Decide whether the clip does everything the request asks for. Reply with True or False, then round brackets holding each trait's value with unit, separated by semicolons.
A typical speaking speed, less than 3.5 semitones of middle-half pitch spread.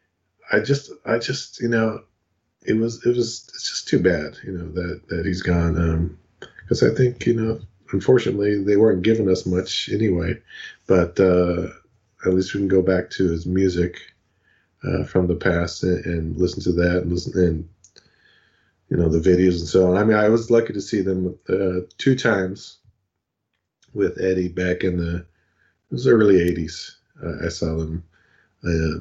True (180 wpm; 2.7 semitones)